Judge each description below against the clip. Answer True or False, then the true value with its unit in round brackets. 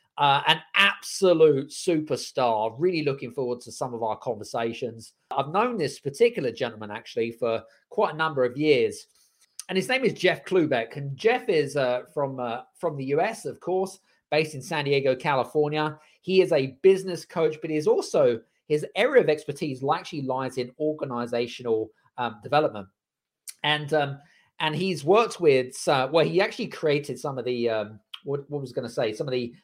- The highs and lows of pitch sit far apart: True (5.8 semitones)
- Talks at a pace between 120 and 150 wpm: False (180 wpm)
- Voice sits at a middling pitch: True (150 Hz)